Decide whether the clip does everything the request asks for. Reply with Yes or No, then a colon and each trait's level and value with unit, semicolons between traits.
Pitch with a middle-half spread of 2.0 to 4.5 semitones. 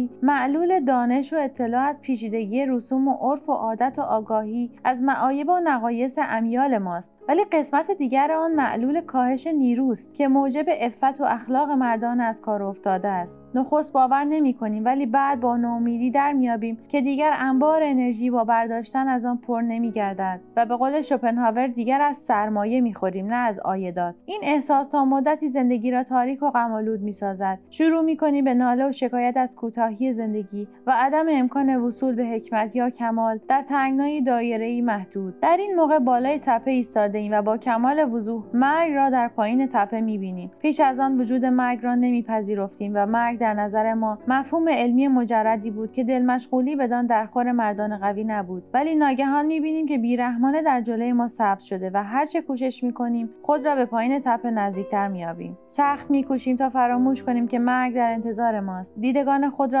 Yes: average, 3.4 semitones